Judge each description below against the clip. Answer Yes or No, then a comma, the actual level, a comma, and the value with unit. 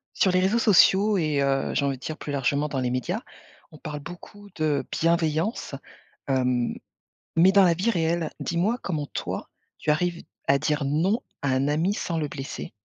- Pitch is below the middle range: No, medium, 155 Hz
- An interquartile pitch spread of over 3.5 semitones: Yes, average, 4.3 semitones